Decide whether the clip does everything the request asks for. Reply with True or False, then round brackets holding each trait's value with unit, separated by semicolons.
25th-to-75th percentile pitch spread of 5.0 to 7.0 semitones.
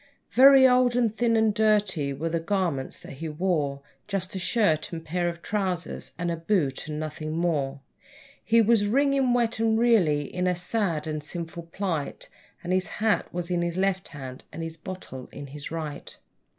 True (5.5 semitones)